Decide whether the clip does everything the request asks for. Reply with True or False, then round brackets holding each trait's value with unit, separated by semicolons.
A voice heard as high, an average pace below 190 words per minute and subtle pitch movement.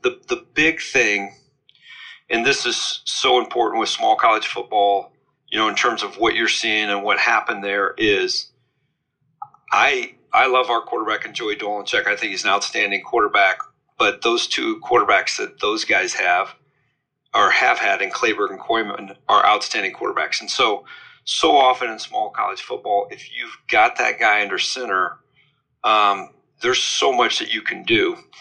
True (375 Hz; 170 wpm; 1.4 semitones)